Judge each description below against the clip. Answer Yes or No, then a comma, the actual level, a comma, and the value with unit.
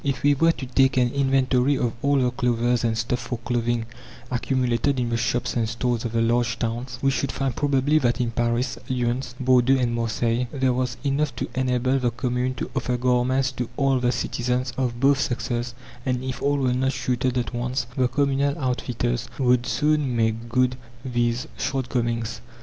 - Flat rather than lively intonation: Yes, narrow, 1.8 semitones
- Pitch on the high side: No, low, 125 Hz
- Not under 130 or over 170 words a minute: No, average, 185 wpm